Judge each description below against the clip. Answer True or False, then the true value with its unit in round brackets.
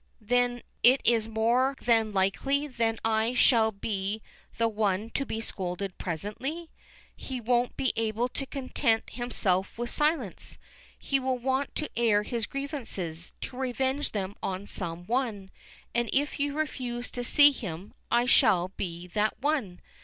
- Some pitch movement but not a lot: True (4.4 semitones)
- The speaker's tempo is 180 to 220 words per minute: False (150 wpm)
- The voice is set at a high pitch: True (230 Hz)